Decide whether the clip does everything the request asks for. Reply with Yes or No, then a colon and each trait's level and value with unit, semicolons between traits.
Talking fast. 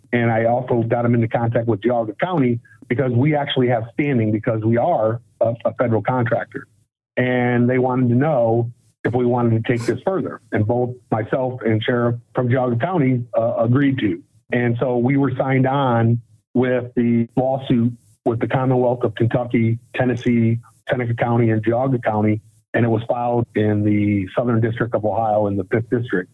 No: average, 180 wpm